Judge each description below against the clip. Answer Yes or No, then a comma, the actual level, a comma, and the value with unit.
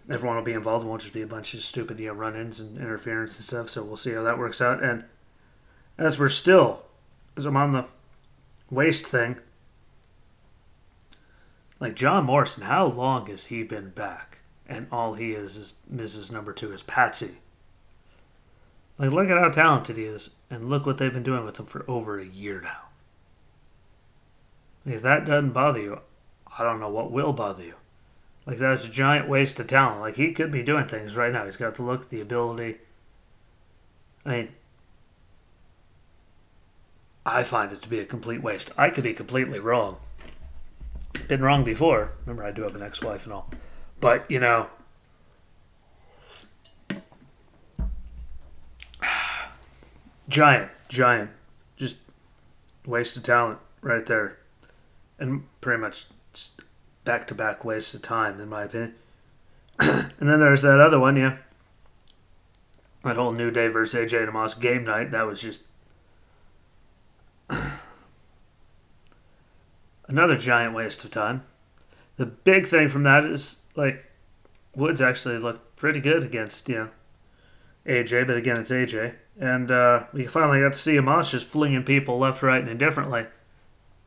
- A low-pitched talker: Yes, low, 115 Hz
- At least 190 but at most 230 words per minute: No, average, 155 wpm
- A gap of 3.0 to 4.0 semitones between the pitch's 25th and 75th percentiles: No, average, 4.4 semitones